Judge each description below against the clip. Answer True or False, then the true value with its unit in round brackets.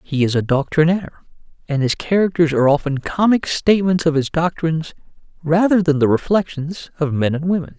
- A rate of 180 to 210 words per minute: False (170 wpm)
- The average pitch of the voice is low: False (160 Hz)